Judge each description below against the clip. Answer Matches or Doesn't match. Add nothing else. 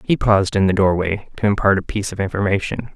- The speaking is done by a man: Matches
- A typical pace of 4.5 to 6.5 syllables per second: Doesn't match